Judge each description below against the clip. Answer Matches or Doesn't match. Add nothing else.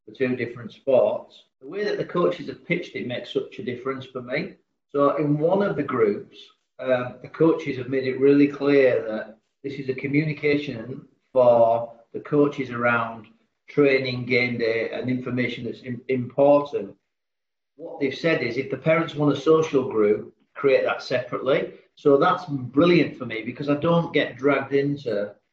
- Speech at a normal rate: Matches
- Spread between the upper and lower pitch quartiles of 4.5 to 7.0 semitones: Doesn't match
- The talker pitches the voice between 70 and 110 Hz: Doesn't match